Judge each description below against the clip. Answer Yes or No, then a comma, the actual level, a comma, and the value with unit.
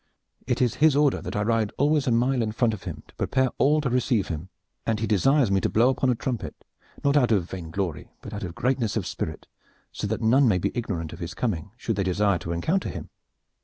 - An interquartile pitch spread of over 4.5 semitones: Yes, average, 5.0 semitones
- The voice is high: No, low, 115 Hz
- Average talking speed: No, fast, 240 wpm